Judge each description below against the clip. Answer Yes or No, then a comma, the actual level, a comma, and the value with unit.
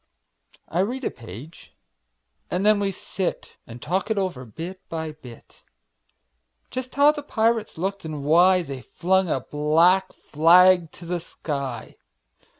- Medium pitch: Yes, medium, 175 Hz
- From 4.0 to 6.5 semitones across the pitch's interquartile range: Yes, average, 4.4 semitones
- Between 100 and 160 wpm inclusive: Yes, average, 145 wpm